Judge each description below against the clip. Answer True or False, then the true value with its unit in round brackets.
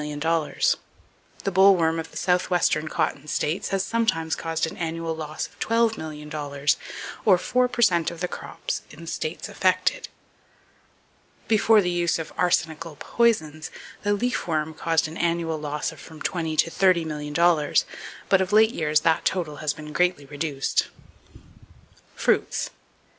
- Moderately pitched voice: True (165 Hz)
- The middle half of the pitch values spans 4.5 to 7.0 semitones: False (3.1 semitones)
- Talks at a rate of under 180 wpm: True (150 wpm)